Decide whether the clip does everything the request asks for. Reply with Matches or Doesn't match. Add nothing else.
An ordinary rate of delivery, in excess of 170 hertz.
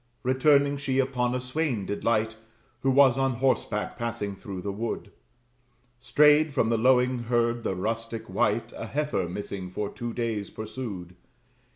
Doesn't match